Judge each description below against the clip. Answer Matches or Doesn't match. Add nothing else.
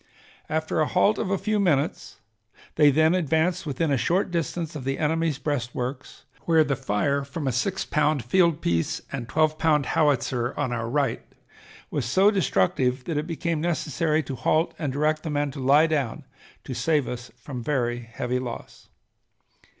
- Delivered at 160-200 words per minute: Matches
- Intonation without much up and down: Doesn't match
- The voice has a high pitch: Doesn't match